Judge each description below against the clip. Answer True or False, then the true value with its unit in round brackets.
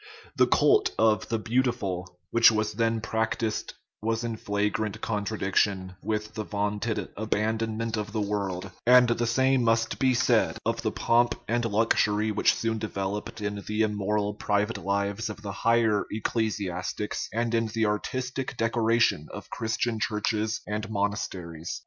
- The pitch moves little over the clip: True (1.9 semitones)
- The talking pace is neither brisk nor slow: True (150 wpm)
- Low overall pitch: True (110 Hz)